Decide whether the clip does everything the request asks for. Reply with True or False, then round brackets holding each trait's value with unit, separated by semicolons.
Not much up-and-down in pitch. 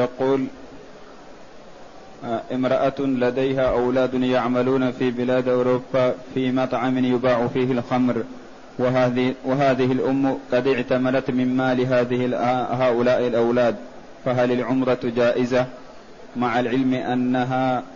True (0.8 semitones)